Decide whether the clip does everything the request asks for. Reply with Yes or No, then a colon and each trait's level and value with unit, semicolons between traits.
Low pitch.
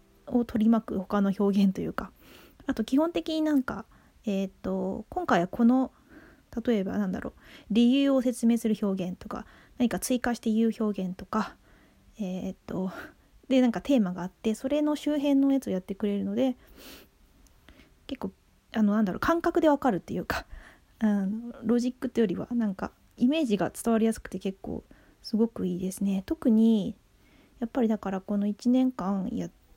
No: high, 225 Hz